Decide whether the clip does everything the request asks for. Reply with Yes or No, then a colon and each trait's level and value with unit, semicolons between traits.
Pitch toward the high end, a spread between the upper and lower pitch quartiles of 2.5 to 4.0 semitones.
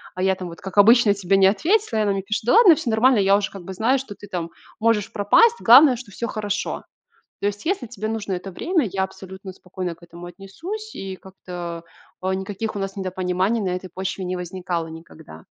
Yes: high, 195 Hz; average, 3.4 semitones